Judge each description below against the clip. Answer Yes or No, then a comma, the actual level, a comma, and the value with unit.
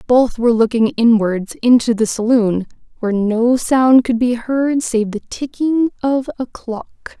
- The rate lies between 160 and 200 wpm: No, average, 150 wpm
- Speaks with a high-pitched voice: Yes, high, 240 Hz